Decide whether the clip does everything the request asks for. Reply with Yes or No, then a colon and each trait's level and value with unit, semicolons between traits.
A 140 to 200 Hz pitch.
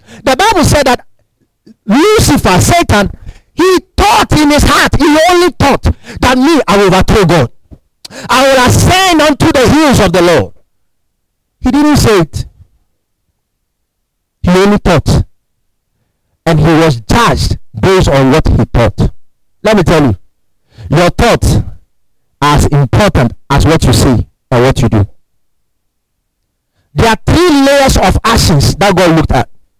Yes: medium, 185 Hz